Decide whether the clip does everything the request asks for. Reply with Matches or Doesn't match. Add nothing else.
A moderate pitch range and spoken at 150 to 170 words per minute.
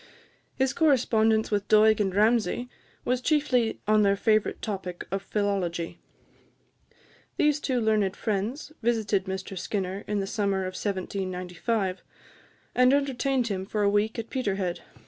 Doesn't match